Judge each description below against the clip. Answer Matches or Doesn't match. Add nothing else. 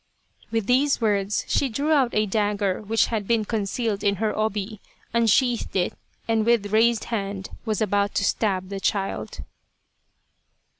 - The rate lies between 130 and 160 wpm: Matches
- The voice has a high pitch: Matches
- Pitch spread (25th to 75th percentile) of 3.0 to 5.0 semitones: Doesn't match